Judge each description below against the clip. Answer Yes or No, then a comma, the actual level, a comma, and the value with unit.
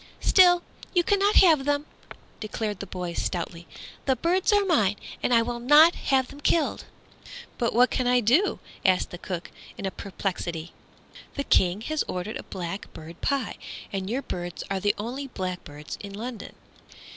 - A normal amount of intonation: No, wide, 7.4 semitones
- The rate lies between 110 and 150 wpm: No, average, 160 wpm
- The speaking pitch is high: Yes, high, 230 Hz